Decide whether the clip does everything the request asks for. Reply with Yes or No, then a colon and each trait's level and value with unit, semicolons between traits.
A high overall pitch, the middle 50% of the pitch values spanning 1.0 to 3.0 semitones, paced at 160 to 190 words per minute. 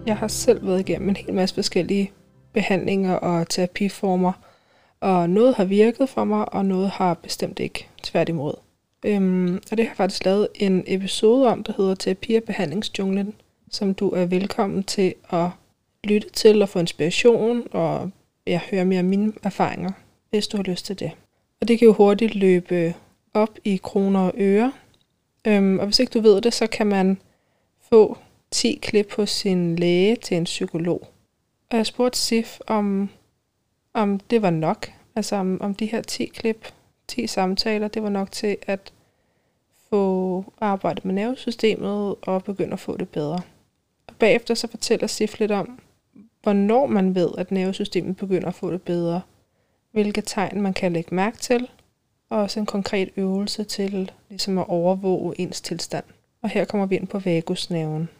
Yes: high, 195 Hz; average, 2.7 semitones; average, 170 wpm